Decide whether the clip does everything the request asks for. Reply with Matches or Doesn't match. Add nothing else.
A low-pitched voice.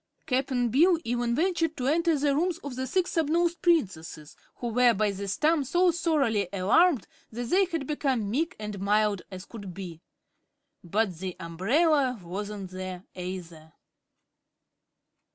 Doesn't match